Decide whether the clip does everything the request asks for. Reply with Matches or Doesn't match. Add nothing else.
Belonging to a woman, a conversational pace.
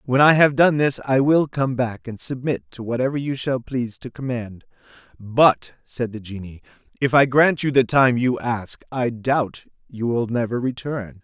Doesn't match